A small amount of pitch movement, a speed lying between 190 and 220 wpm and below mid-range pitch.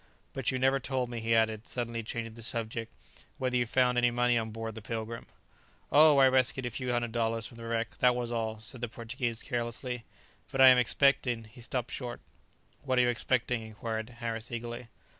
Yes: narrow, 1.6 semitones; average, 200 wpm; low, 120 Hz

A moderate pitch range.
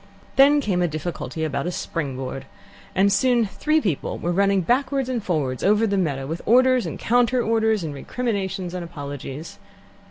No: wide, 7.1 semitones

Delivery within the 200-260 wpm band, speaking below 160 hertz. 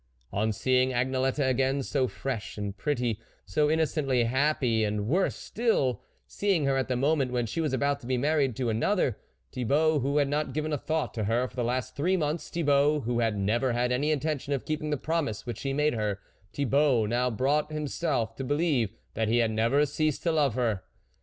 Yes: fast, 205 wpm; low, 135 Hz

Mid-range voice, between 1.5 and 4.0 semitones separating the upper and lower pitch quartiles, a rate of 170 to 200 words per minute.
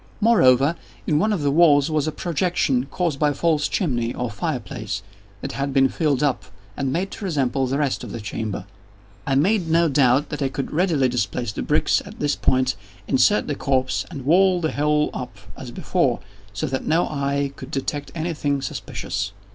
Yes: medium, 145 Hz; average, 3.7 semitones; average, 195 wpm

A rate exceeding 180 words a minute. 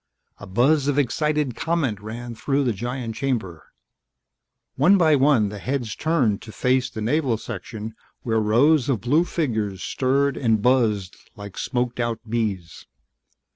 No: average, 145 wpm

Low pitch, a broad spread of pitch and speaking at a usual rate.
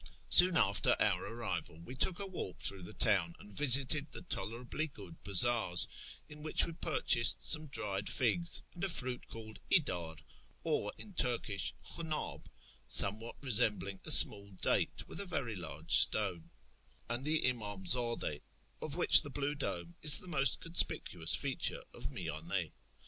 Yes: low, 115 Hz; wide, 7.7 semitones; average, 150 wpm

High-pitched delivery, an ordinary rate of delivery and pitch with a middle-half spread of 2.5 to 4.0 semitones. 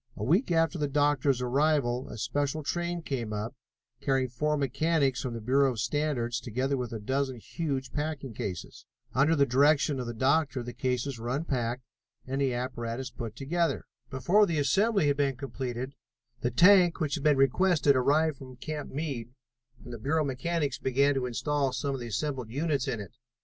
No: low, 135 Hz; average, 180 wpm; average, 3.3 semitones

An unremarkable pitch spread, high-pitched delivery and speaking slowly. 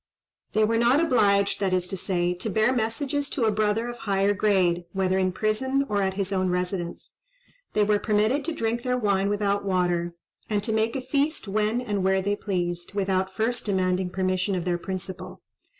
No: average, 3.1 semitones; high, 200 Hz; average, 195 wpm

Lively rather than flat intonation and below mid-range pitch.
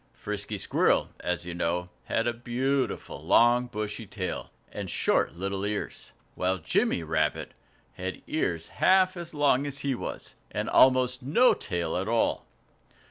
Yes: wide, 6.1 semitones; low, 110 Hz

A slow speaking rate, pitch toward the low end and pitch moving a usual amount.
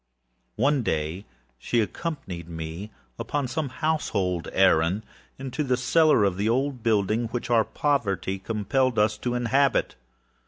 No: slow, 130 wpm; low, 115 Hz; wide, 5.8 semitones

